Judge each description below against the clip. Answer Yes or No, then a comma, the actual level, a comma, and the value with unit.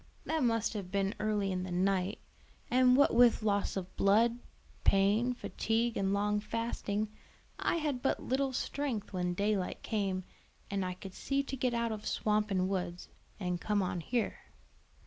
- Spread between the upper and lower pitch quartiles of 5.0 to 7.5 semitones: No, average, 3.6 semitones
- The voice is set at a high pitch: Yes, high, 210 Hz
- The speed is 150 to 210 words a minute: Yes, average, 165 wpm